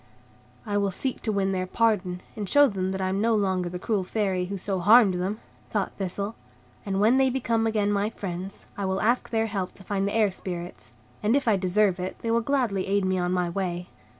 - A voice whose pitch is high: Yes, high, 200 Hz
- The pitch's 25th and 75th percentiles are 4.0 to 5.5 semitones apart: No, average, 2.9 semitones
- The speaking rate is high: Yes, fast, 230 wpm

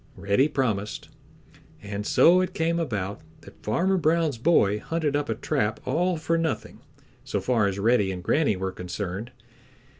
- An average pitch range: No, wide, 8.2 semitones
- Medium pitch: No, low, 120 Hz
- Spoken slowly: No, average, 155 wpm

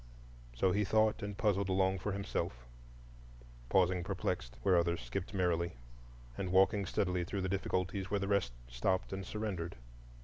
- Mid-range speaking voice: No, very low, 95 Hz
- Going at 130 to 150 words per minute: Yes, average, 145 wpm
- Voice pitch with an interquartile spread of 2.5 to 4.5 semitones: Yes, average, 3.1 semitones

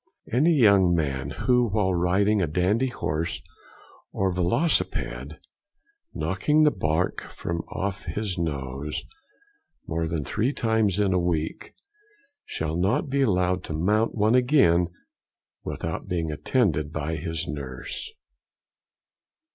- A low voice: Yes, very low, 90 Hz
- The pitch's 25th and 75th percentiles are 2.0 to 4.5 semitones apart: No, average, 5.2 semitones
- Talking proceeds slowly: Yes, slow, 120 wpm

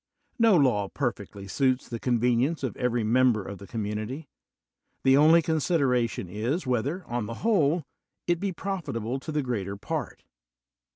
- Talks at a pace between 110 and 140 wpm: No, average, 155 wpm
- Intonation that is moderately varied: No, wide, 5.8 semitones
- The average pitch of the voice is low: Yes, low, 125 Hz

